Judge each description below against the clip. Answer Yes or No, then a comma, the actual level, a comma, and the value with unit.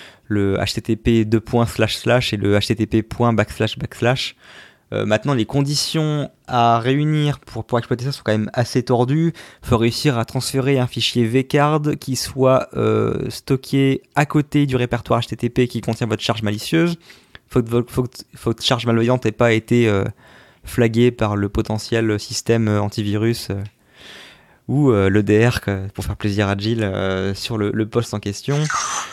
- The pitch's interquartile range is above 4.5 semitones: No, average, 3.3 semitones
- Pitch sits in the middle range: No, low, 115 Hz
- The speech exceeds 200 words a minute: No, average, 165 wpm